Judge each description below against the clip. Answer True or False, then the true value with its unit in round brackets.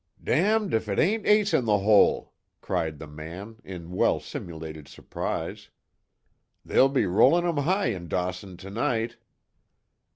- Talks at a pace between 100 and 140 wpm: True (135 wpm)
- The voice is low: True (105 Hz)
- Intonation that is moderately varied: False (8.8 semitones)